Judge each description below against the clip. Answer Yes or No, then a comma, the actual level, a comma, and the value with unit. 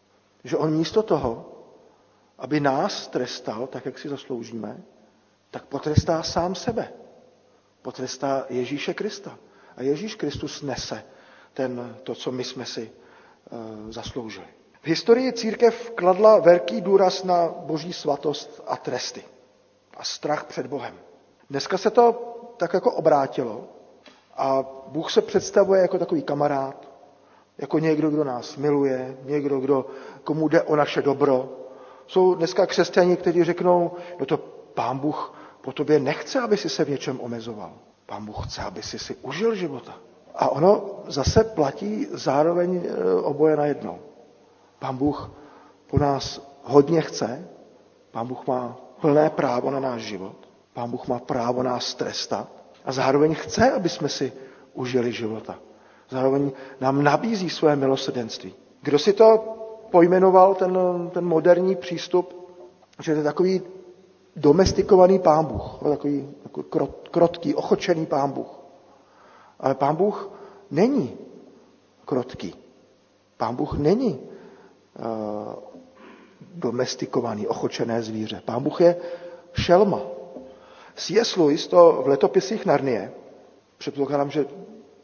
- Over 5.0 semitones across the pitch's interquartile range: Yes, wide, 5.6 semitones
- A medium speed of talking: Yes, average, 130 wpm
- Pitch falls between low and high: Yes, medium, 150 Hz